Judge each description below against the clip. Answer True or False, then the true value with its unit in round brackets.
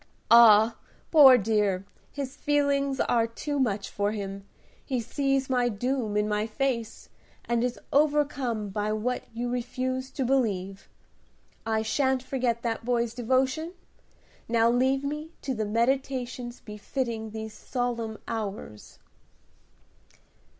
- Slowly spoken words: True (120 wpm)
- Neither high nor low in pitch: False (240 Hz)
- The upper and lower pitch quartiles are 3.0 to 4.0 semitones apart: True (3.3 semitones)